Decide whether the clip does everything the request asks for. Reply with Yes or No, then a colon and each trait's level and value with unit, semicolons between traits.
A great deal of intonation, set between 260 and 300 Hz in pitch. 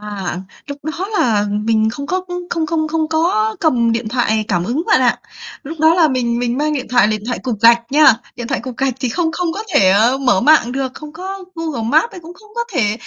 Yes: wide, 5.7 semitones; very high, 270 Hz